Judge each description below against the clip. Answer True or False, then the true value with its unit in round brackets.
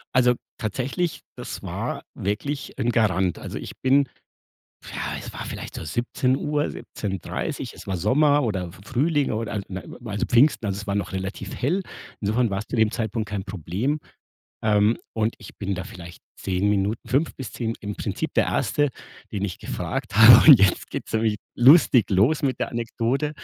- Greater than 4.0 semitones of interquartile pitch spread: True (4.8 semitones)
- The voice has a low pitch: True (110 Hz)